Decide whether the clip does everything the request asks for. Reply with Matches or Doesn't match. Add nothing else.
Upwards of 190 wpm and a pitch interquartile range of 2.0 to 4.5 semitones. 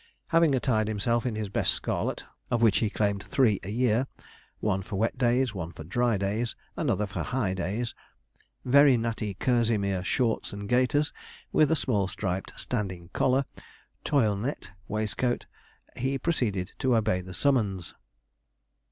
Doesn't match